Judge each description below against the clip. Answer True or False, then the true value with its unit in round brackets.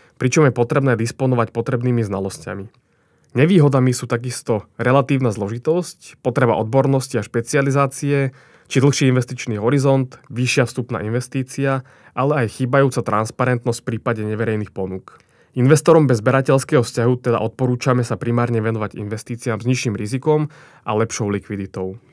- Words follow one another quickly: False (125 wpm)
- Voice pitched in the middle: False (125 Hz)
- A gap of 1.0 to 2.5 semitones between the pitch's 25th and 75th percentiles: False (2.9 semitones)